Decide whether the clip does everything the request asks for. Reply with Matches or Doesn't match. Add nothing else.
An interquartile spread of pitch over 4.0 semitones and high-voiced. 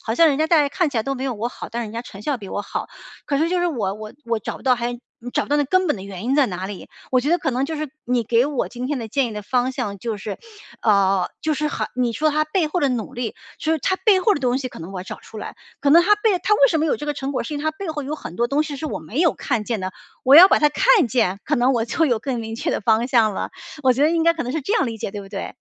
Matches